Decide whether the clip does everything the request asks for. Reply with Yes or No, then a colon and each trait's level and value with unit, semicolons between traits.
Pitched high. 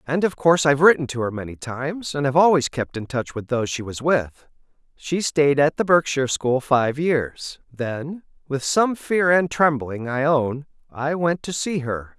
No: medium, 145 Hz